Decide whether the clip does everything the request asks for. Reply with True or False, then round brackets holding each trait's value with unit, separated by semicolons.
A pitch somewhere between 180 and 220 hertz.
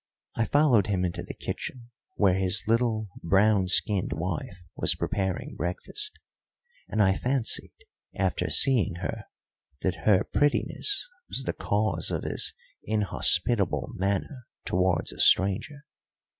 False (100 Hz)